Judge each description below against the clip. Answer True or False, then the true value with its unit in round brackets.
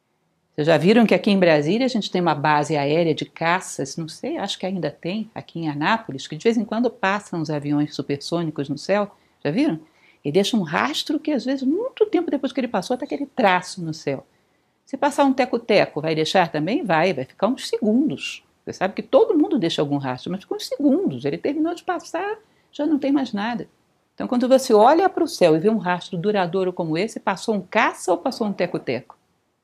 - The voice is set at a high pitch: True (205 Hz)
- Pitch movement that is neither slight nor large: False (8.3 semitones)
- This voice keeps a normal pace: False (220 wpm)